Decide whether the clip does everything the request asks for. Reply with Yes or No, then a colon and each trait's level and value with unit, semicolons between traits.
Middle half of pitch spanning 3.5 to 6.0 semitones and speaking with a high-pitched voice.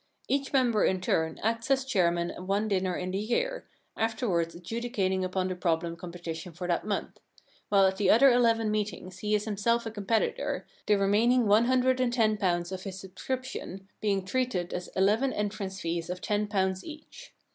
Yes: average, 3.9 semitones; high, 205 Hz